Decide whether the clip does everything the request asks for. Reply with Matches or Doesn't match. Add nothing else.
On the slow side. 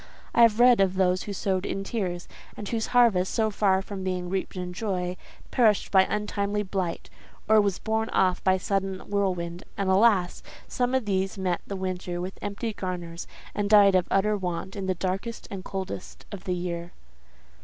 Doesn't match